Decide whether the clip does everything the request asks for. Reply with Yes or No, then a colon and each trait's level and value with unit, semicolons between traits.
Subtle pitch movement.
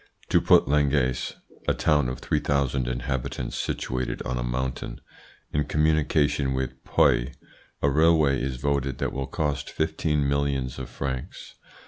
Yes: narrow, 2.2 semitones